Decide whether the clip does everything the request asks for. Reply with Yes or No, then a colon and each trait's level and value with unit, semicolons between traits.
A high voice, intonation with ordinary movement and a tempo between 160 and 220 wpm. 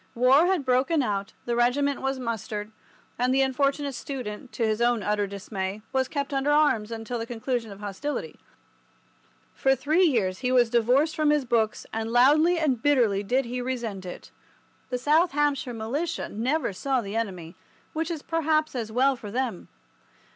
Yes: very high, 250 Hz; average, 4.3 semitones; average, 170 wpm